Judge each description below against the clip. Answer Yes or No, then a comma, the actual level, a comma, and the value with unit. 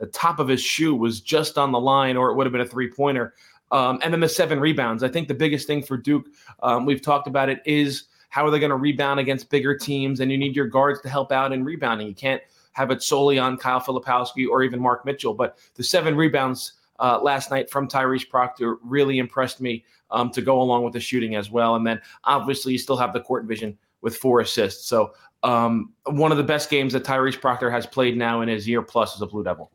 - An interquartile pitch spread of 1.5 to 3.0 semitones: Yes, narrow, 2.5 semitones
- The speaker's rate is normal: No, fast, 245 wpm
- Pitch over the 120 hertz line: Yes, low, 130 Hz